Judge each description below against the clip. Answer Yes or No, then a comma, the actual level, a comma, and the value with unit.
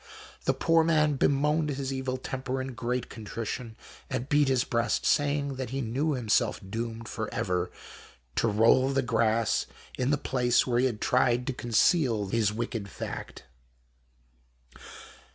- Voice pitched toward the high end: No, low, 125 Hz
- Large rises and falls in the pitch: No, average, 3.0 semitones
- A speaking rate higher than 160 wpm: No, average, 150 wpm